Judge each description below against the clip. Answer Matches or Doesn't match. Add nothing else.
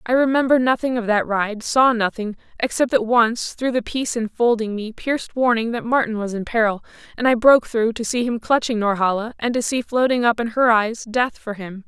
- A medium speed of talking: Doesn't match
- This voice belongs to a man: Doesn't match